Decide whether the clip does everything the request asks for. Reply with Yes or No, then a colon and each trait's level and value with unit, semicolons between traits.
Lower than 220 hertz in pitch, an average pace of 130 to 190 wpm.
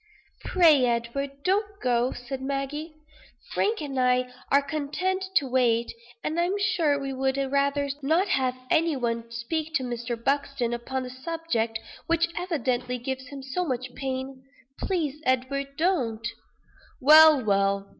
No: very high, 270 Hz; average, 140 wpm